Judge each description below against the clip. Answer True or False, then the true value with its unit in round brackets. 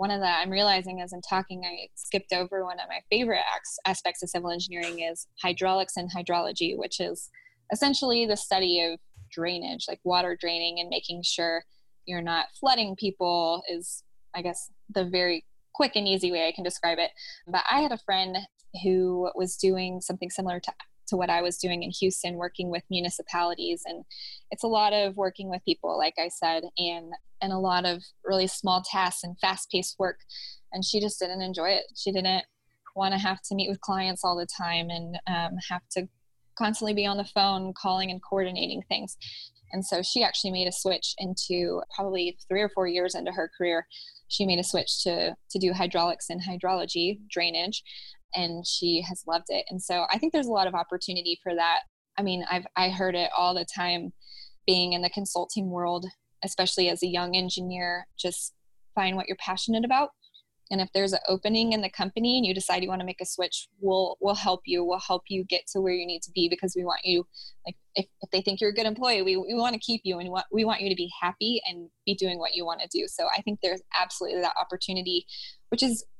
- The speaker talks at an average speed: False (215 wpm)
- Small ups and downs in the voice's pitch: True (1.8 semitones)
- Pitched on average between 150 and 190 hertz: True (185 Hz)